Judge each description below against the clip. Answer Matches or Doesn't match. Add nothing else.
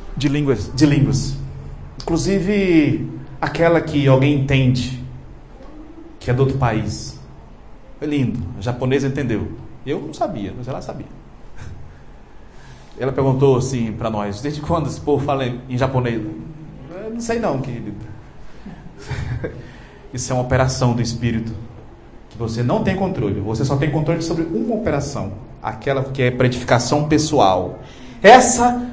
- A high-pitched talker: Doesn't match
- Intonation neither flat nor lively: Matches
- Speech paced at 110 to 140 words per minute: Matches